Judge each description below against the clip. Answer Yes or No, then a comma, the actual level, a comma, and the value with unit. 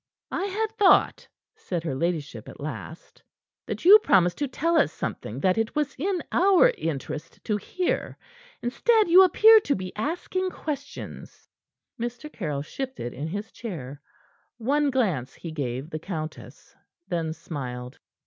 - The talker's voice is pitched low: No, high, 210 Hz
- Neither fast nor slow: Yes, average, 145 wpm